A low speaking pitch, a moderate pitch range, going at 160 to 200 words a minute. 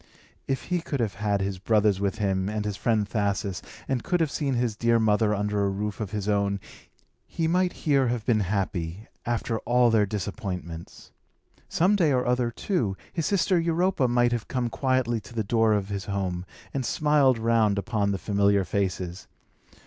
Yes: low, 110 Hz; average, 3.8 semitones; average, 185 wpm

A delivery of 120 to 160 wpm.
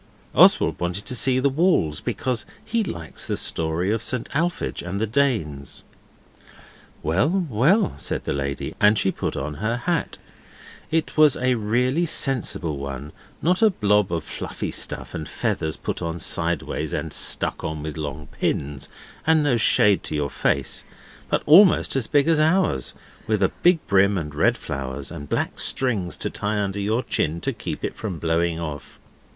No: average, 170 wpm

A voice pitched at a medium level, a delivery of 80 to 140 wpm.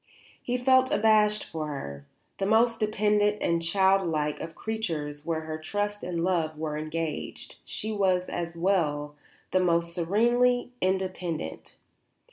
Yes: medium, 180 Hz; slow, 135 wpm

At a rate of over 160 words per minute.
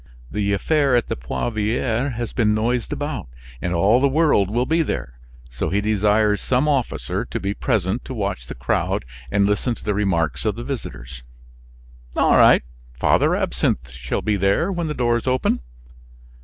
Yes: average, 170 wpm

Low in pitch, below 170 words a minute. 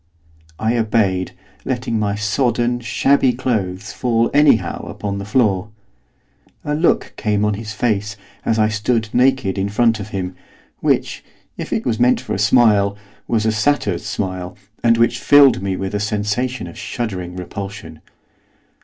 Yes: low, 110 Hz; average, 155 wpm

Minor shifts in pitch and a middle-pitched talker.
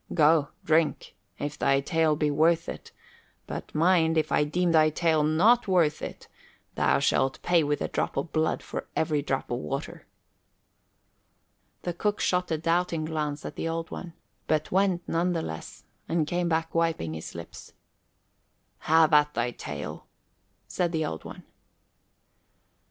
Yes: narrow, 2.3 semitones; medium, 160 Hz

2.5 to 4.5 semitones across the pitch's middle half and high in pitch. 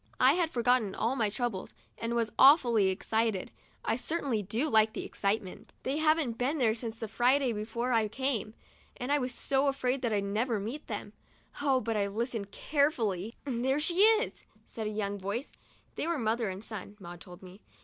Yes: average, 4.1 semitones; high, 230 Hz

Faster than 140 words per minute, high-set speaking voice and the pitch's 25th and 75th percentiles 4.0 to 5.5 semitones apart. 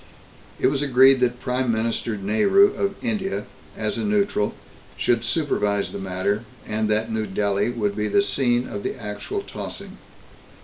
No: average, 160 wpm; low, 115 Hz; average, 5.2 semitones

